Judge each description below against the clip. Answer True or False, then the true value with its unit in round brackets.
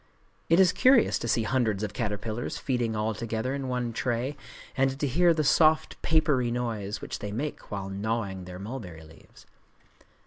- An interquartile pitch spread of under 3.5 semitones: False (4.6 semitones)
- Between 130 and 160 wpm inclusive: False (170 wpm)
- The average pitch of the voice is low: True (120 Hz)